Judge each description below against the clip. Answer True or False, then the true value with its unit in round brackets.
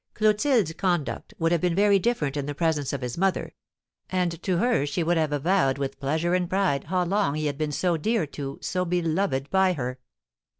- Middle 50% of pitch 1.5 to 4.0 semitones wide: False (4.6 semitones)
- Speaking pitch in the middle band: True (170 Hz)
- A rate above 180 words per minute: True (205 wpm)